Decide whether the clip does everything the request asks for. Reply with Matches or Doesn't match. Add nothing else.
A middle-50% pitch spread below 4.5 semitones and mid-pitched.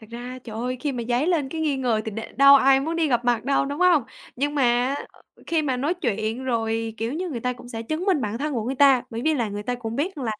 Doesn't match